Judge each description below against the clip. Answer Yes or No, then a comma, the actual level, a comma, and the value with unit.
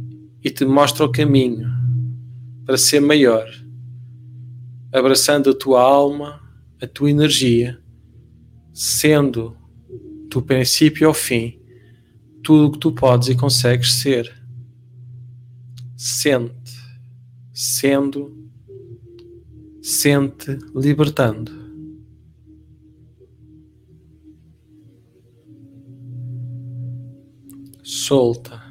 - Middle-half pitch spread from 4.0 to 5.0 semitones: No, average, 2.7 semitones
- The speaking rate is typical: No, slow, 70 wpm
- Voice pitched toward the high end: No, low, 125 Hz